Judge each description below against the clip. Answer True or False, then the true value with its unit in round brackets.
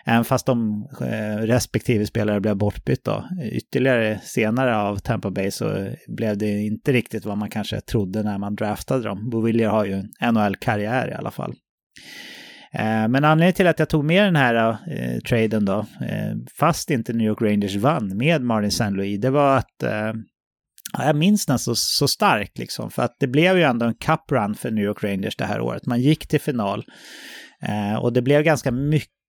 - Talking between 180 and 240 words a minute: True (185 wpm)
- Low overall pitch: True (115 Hz)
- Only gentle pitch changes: False (4.0 semitones)